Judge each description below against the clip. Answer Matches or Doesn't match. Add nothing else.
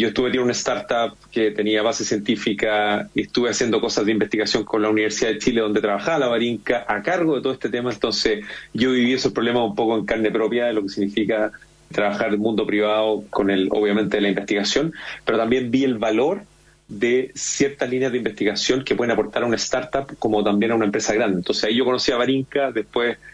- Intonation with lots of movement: Doesn't match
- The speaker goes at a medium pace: Doesn't match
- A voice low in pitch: Matches